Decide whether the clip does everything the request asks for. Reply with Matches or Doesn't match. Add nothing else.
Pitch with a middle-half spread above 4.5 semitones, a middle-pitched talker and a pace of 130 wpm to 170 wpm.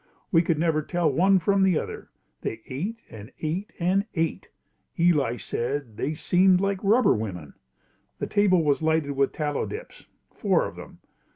Matches